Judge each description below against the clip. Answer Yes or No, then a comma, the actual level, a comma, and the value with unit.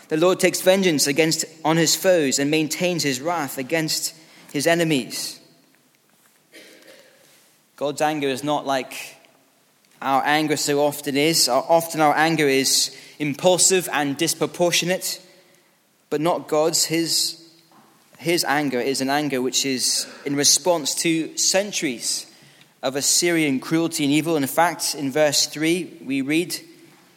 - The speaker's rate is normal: No, slow, 130 wpm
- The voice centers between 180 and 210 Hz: No, medium, 155 Hz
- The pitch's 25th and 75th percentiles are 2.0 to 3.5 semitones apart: Yes, average, 3.0 semitones